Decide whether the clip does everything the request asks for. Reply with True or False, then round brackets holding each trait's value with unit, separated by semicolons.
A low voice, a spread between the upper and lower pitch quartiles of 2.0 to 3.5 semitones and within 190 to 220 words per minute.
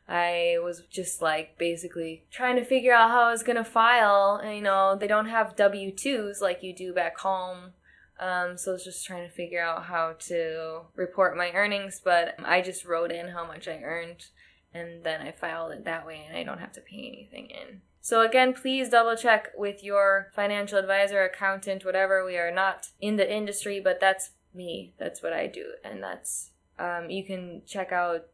False (190 Hz; 2.9 semitones; 200 wpm)